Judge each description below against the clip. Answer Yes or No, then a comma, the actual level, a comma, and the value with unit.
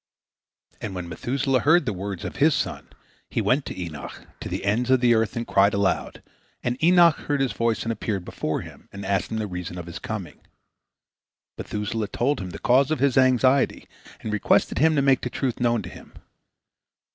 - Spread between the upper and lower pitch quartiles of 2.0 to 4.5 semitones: No, average, 5.1 semitones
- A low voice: Yes, low, 120 Hz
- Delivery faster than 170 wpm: Yes, fast, 205 wpm